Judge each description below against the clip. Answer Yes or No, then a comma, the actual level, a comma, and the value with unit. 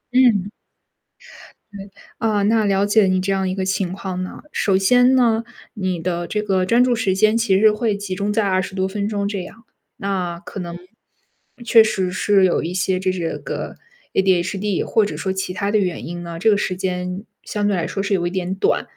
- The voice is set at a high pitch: Yes, high, 195 Hz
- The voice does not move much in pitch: Yes, narrow, 2.1 semitones